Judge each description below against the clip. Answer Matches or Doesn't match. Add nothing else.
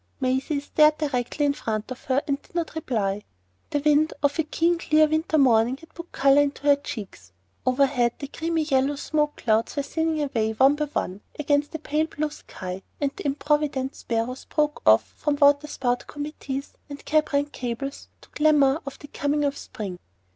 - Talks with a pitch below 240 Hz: Doesn't match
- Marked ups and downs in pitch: Doesn't match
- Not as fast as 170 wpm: Doesn't match